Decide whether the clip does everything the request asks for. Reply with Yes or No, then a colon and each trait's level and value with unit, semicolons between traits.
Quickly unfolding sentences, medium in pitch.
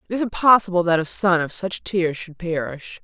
Yes: fast, 215 wpm; medium, 175 Hz